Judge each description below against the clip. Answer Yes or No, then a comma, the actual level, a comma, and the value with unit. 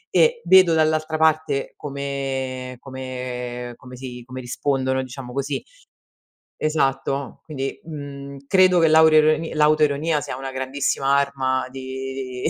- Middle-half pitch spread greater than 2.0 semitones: Yes, average, 2.7 semitones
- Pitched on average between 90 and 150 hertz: Yes, low, 135 Hz